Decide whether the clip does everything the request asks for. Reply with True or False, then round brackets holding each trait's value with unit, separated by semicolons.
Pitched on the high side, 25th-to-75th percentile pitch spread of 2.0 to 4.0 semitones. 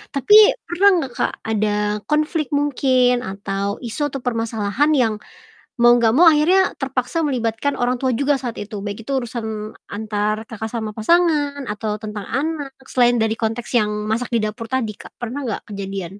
False (240 Hz; 4.5 semitones)